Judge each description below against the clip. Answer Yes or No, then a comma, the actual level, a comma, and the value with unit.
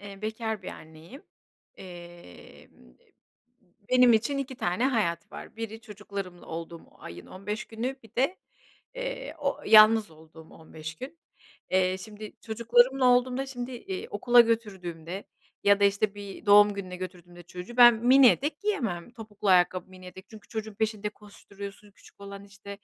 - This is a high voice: Yes, high, 210 Hz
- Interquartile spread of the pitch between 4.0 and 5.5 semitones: Yes, average, 4.4 semitones